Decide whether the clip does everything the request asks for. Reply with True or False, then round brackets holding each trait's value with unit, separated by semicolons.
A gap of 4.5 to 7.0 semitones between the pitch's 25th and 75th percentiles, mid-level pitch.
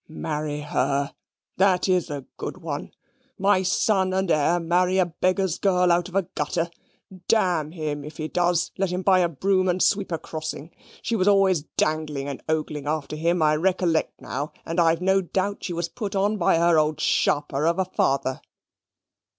False (3.4 semitones; 170 Hz)